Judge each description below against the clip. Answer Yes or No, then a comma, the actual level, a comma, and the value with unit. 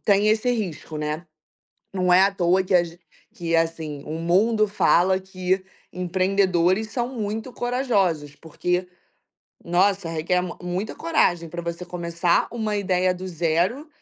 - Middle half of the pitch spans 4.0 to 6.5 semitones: No, average, 2.9 semitones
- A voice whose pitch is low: No, medium, 180 Hz